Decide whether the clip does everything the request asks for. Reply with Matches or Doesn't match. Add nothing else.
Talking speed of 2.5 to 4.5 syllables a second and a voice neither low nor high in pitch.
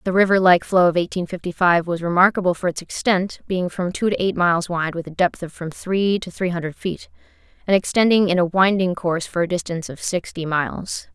Doesn't match